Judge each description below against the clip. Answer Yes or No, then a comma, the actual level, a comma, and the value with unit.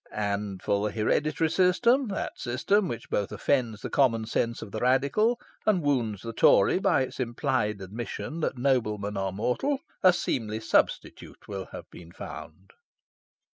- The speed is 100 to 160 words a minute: Yes, average, 155 wpm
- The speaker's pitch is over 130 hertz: No, low, 120 Hz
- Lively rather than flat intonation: Yes, wide, 6.5 semitones